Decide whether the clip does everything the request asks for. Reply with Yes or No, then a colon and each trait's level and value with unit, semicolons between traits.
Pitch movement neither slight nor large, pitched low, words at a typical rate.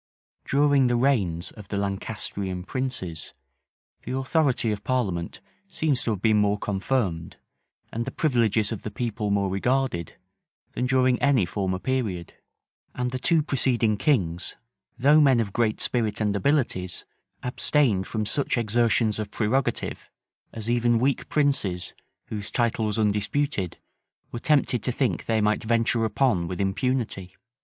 Yes: average, 4.4 semitones; low, 115 Hz; average, 145 wpm